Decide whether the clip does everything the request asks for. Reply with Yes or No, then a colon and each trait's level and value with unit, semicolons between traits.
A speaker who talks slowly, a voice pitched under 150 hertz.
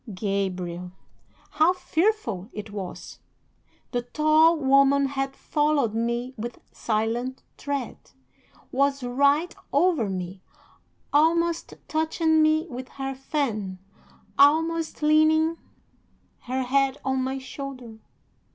No: slow, 100 wpm; very high, 270 Hz